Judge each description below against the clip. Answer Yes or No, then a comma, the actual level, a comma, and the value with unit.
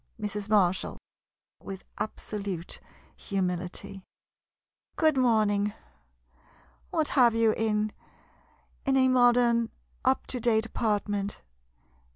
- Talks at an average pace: No, slow, 95 wpm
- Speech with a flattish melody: No, average, 3.2 semitones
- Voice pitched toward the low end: No, high, 215 Hz